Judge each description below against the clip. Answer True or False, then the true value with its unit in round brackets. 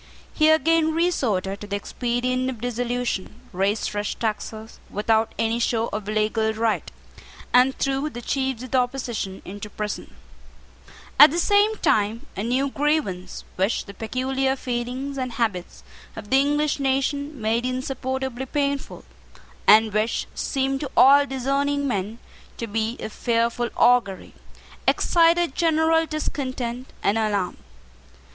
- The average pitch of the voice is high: True (245 Hz)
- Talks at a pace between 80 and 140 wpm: True (135 wpm)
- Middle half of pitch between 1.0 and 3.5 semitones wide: False (4.0 semitones)